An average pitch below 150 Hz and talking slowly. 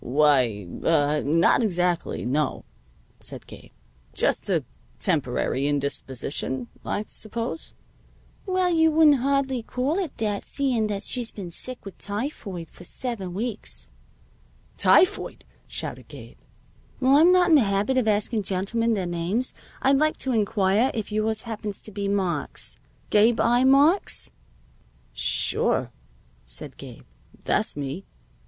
No: high, 215 Hz; slow, 130 wpm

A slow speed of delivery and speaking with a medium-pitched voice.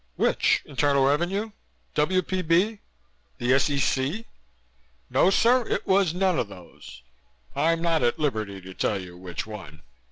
Yes: slow, 130 wpm; medium, 145 Hz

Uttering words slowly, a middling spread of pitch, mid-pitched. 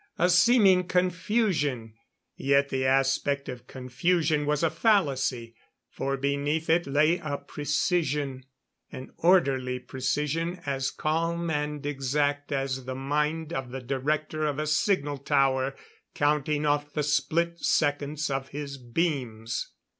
Yes: slow, 125 wpm; average, 3.0 semitones; medium, 145 Hz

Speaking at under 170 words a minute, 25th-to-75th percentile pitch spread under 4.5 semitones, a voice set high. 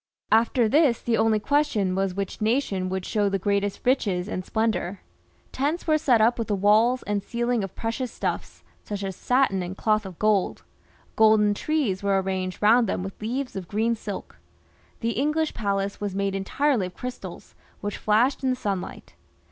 No: average, 180 wpm; average, 3.8 semitones; high, 215 Hz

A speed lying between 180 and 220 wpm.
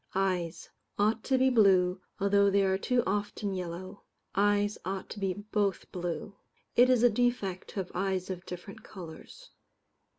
No: average, 160 wpm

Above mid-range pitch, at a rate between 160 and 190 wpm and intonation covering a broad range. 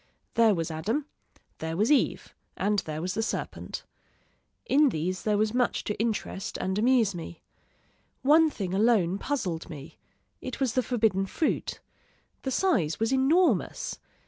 No: high, 215 Hz; average, 145 wpm; wide, 6.1 semitones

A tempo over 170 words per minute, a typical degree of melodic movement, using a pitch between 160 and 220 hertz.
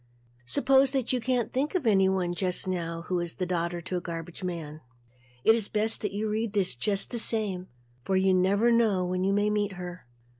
Yes: average, 200 wpm; average, 3.6 semitones; high, 190 Hz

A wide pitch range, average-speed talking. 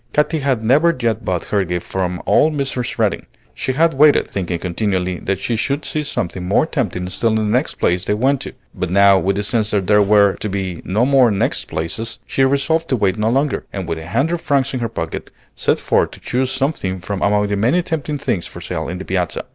No: wide, 6.3 semitones; fast, 230 wpm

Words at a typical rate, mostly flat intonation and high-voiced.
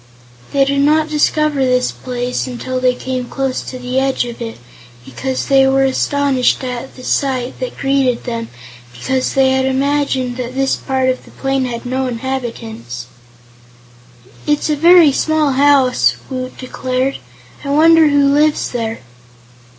Yes: average, 150 wpm; narrow, 1.9 semitones; very high, 265 Hz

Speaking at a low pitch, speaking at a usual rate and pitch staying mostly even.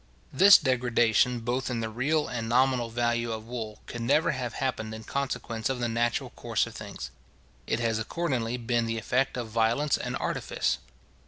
Yes: low, 120 Hz; average, 175 wpm; narrow, 2.1 semitones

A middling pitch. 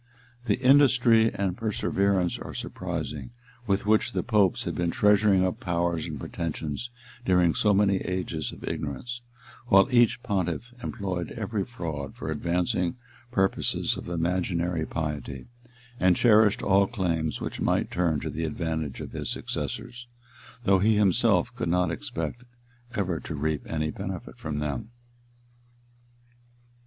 No: very low, 90 Hz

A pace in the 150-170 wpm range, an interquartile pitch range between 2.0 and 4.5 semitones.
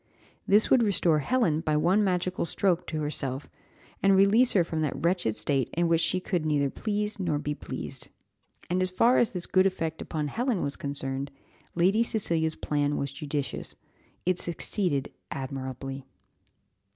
No: average, 160 wpm; average, 4.9 semitones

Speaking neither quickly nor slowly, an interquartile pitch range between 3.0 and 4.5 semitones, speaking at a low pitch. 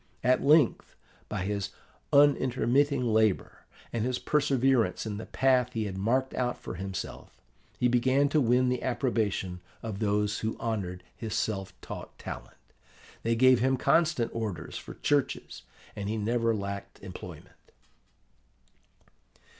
No: slow, 130 wpm; average, 3.8 semitones; low, 115 Hz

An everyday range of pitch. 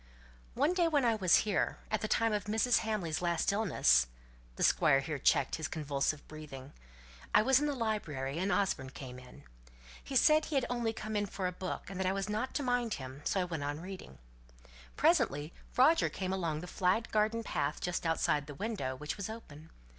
No: wide, 6.9 semitones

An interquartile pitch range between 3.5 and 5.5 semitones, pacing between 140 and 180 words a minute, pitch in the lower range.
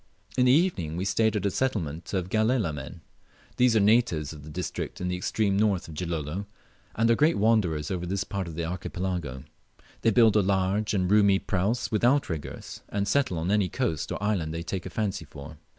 No: average, 4.4 semitones; average, 200 wpm; very low, 95 Hz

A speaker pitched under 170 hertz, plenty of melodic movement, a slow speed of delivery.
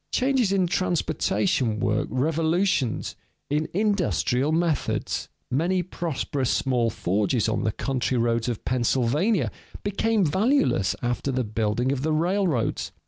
Yes: medium, 140 Hz; wide, 7.5 semitones; slow, 120 wpm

